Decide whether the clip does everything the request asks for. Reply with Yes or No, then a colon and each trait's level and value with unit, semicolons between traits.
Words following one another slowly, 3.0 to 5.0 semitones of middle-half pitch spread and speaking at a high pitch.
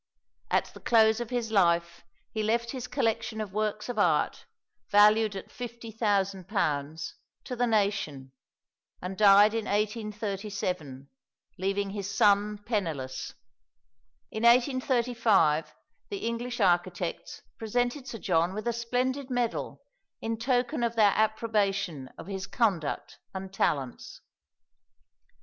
Yes: slow, 120 wpm; average, 3.5 semitones; high, 210 Hz